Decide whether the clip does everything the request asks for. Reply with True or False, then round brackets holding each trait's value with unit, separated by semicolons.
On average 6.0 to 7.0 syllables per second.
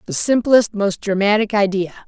False (5.0 syllables/s)